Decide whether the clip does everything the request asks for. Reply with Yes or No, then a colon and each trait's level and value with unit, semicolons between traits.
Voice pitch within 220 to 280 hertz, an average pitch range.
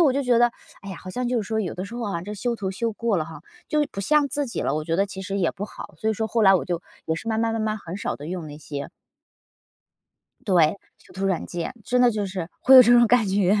No: high, 205 Hz; average, 4.3 semitones